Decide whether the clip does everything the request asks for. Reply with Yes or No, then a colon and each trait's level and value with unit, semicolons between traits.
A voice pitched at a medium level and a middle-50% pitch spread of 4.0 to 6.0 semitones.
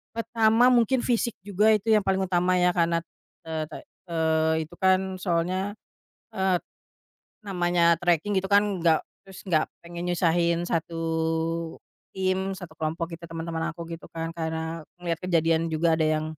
No: medium, 175 Hz; narrow, 2.5 semitones